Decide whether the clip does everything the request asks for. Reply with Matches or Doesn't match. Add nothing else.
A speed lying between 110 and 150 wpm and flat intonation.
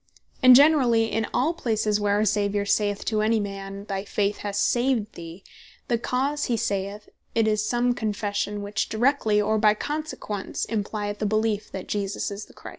Doesn't match